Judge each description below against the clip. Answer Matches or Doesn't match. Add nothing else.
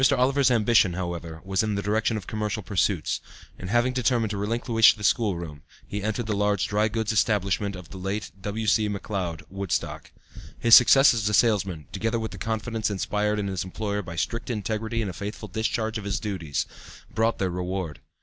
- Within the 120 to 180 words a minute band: Doesn't match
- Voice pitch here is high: Doesn't match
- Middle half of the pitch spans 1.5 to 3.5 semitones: Matches